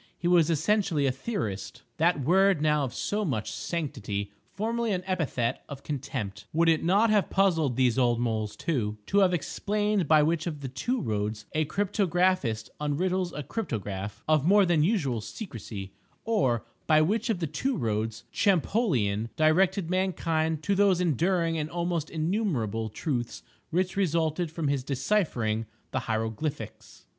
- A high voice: No, medium, 155 Hz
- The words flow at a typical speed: Yes, average, 150 wpm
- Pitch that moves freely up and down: Yes, wide, 7.5 semitones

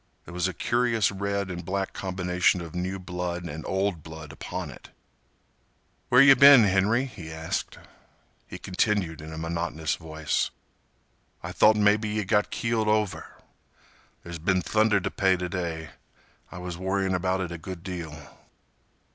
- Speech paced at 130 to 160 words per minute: Yes, average, 155 wpm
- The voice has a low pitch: Yes, very low, 95 Hz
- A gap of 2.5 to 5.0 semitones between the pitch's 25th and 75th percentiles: Yes, average, 3.3 semitones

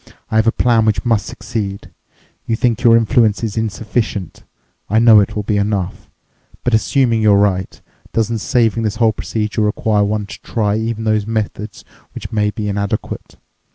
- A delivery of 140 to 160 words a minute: No, average, 170 wpm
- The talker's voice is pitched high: No, low, 110 Hz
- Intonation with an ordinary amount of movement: No, narrow, 1.7 semitones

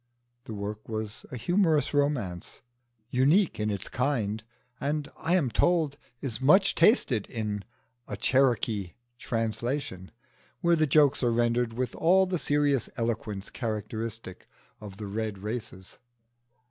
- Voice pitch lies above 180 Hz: No, low, 120 Hz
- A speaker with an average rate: No, slow, 130 wpm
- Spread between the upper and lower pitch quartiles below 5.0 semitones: No, wide, 5.4 semitones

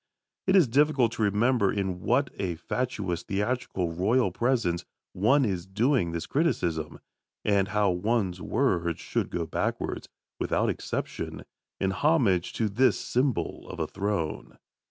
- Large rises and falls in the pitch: Yes, wide, 5.8 semitones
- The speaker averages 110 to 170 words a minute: Yes, slow, 135 wpm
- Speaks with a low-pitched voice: Yes, low, 105 Hz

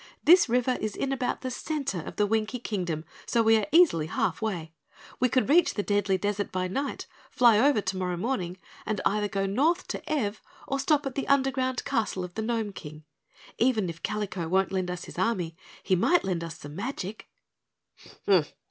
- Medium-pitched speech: No, high, 210 Hz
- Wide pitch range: Yes, wide, 5.7 semitones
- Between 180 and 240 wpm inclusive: Yes, average, 190 wpm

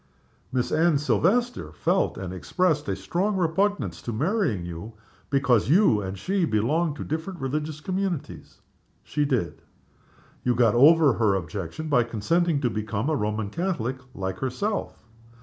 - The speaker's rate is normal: Yes, average, 145 wpm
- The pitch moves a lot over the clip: Yes, wide, 8.1 semitones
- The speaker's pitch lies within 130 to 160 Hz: Yes, medium, 140 Hz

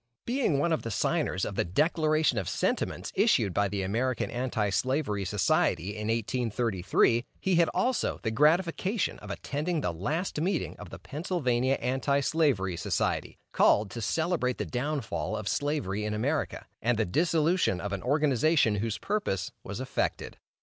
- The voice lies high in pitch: No, low, 130 Hz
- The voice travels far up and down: Yes, wide, 6.9 semitones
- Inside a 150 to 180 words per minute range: Yes, average, 155 wpm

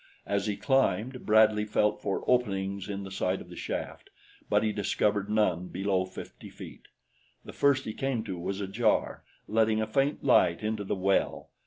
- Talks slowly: No, average, 175 wpm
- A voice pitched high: No, low, 105 Hz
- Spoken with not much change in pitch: Yes, narrow, 2.2 semitones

